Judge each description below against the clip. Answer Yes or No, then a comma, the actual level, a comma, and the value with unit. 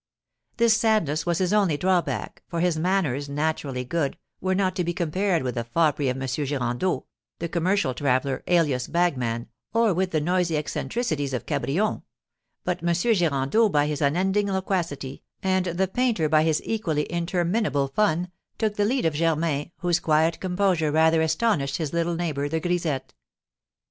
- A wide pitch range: No, average, 4.3 semitones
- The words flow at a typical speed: Yes, average, 160 wpm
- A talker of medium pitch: Yes, medium, 165 Hz